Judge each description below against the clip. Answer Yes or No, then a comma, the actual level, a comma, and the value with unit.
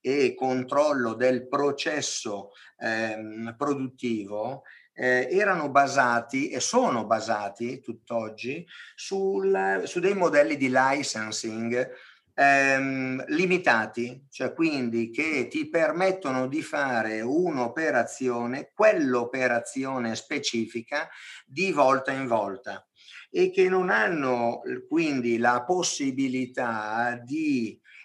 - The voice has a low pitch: Yes, low, 130 Hz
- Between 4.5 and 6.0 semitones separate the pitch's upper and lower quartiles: Yes, average, 4.8 semitones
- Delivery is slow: Yes, slow, 90 wpm